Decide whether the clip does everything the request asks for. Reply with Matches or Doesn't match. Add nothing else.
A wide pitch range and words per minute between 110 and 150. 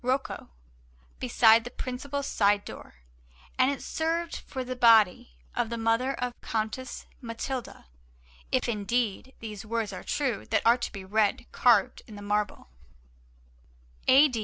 Doesn't match